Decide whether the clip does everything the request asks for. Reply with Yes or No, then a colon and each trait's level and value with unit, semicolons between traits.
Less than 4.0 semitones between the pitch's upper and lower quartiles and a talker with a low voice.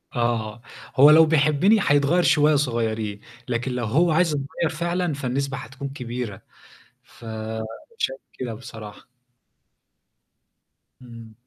No: average, 4.8 semitones; low, 130 Hz